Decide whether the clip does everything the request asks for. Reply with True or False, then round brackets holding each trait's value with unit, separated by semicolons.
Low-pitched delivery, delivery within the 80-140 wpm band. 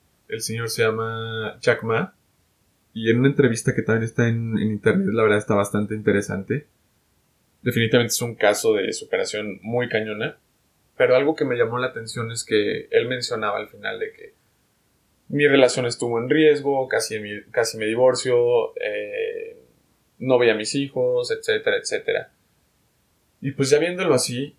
False (125 Hz; 165 wpm)